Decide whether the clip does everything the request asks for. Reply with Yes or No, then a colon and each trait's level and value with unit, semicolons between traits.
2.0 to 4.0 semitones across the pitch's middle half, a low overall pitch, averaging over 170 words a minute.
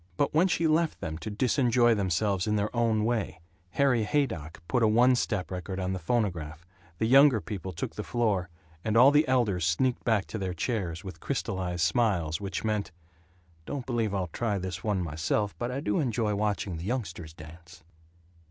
No: average, 4.9 semitones; low, 105 Hz; average, 185 wpm